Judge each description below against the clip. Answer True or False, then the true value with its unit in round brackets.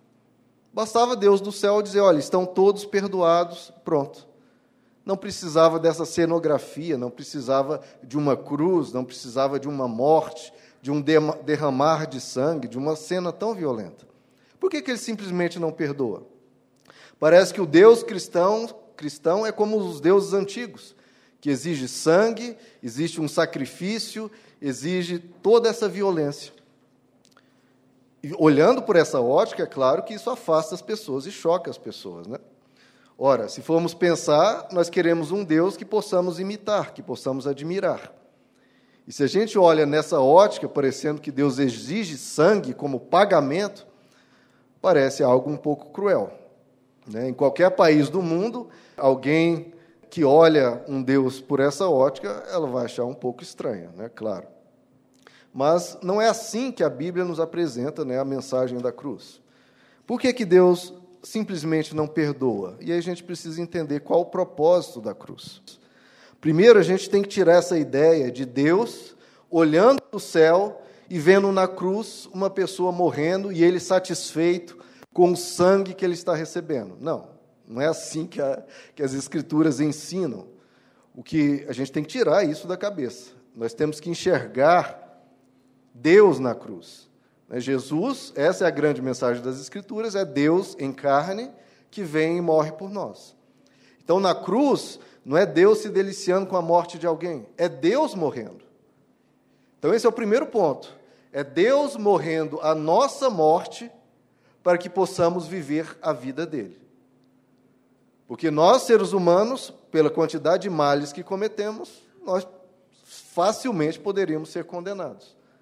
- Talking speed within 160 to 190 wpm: False (150 wpm)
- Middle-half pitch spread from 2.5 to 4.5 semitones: False (5.0 semitones)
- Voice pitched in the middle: True (170 Hz)